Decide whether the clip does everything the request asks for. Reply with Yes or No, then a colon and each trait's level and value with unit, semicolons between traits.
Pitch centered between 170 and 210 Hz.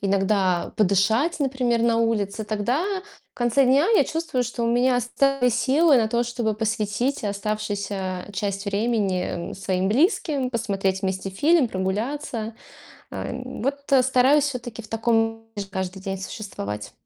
No: high, 225 Hz